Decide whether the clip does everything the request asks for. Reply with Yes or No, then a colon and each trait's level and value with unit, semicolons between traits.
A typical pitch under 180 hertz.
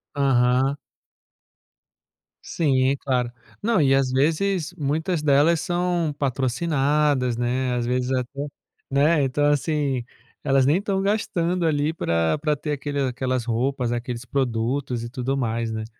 Yes: low, 135 Hz